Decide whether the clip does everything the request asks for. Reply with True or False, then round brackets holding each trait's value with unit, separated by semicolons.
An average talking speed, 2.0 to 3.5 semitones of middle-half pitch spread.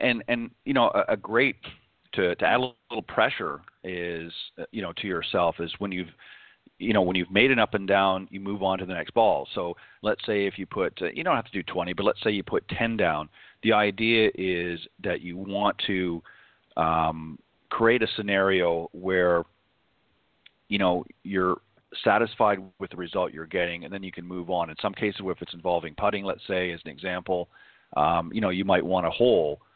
False (210 wpm; 2.5 semitones)